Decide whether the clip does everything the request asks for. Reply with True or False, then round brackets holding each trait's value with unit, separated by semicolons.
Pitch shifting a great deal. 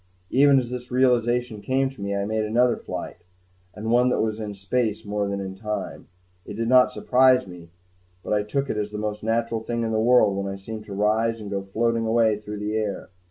False (2.5 semitones)